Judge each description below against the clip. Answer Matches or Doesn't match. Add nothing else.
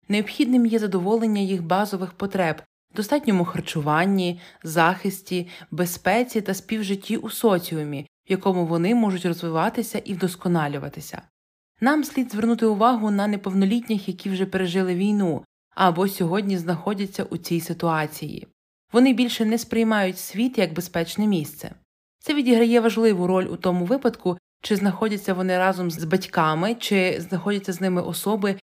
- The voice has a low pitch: Doesn't match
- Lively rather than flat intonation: Doesn't match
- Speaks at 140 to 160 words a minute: Doesn't match